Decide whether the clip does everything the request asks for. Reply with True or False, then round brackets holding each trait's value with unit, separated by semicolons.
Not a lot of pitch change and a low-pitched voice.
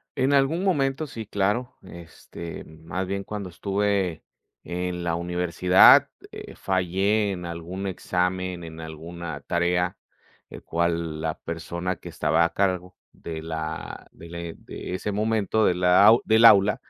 False (3.0 semitones; 90 Hz)